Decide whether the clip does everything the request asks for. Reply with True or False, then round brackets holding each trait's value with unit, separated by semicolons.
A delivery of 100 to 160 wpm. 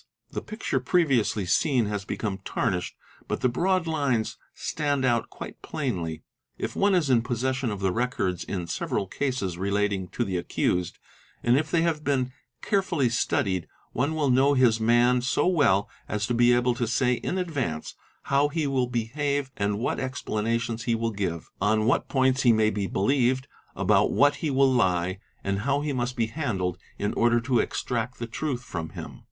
False (185 wpm)